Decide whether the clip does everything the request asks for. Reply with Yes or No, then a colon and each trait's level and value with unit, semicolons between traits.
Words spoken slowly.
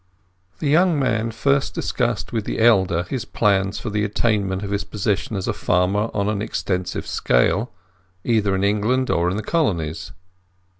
No: average, 160 wpm